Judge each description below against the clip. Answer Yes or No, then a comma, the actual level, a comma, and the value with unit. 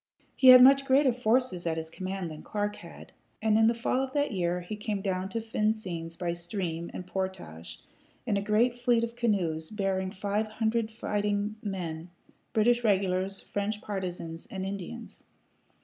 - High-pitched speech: Yes, high, 205 Hz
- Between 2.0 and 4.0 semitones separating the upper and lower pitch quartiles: Yes, average, 3.7 semitones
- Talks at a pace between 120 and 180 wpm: Yes, average, 165 wpm